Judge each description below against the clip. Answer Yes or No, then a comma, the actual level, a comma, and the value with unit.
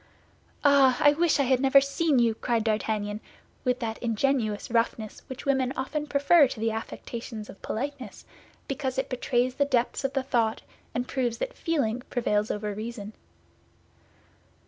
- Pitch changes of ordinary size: Yes, average, 3.7 semitones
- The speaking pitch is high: Yes, very high, 250 Hz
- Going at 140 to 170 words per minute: Yes, average, 155 wpm